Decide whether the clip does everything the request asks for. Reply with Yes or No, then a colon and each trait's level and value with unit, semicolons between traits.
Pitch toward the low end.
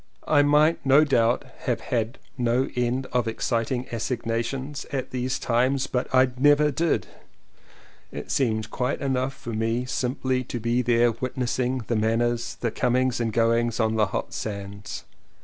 Yes: low, 125 Hz